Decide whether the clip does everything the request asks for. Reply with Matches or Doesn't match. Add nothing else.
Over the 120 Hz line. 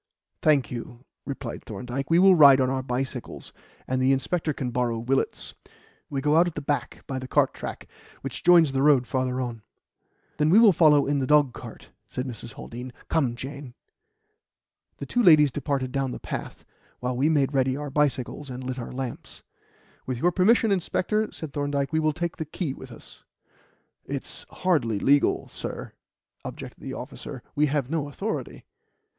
Matches